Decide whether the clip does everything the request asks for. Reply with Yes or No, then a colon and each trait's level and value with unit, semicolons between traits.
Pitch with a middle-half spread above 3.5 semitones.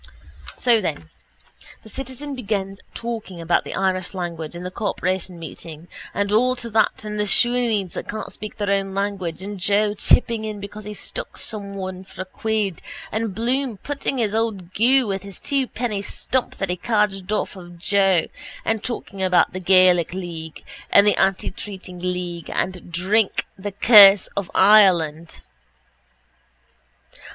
No: average, 3.0 semitones